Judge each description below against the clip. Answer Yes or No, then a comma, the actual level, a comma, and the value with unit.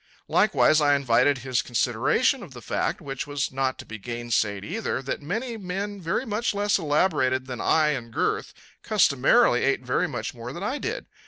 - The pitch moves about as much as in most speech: No, wide, 8.0 semitones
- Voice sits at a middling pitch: Yes, medium, 145 Hz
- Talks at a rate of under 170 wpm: No, average, 180 wpm